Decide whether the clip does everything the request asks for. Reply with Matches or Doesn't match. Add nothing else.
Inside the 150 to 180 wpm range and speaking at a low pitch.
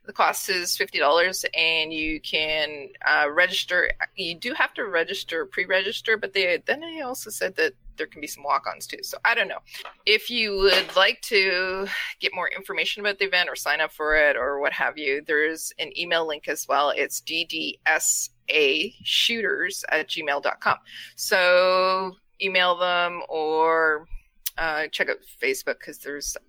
Doesn't match